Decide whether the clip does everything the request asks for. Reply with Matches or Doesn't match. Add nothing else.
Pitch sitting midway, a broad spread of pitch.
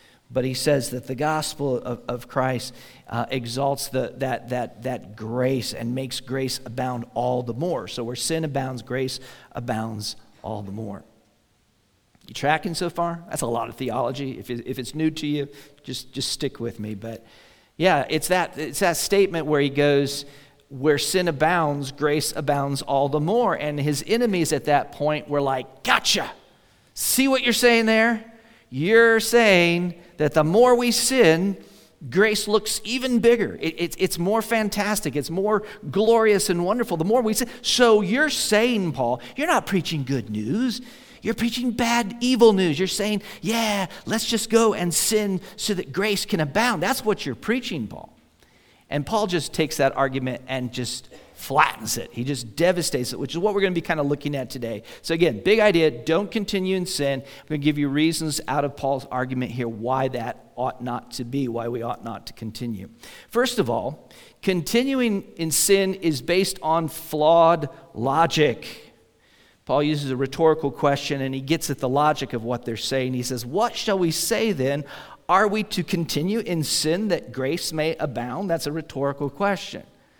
Matches